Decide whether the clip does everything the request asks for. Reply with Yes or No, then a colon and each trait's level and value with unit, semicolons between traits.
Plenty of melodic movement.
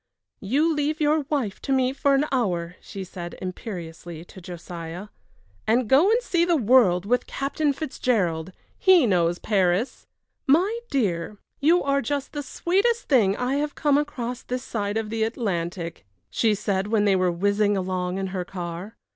Yes: wide, 7.3 semitones